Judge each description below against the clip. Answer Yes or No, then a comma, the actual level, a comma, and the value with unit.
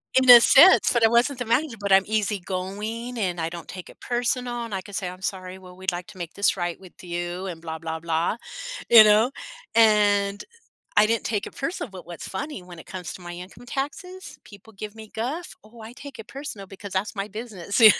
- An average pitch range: Yes, average, 4.4 semitones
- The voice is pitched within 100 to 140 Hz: No, high, 205 Hz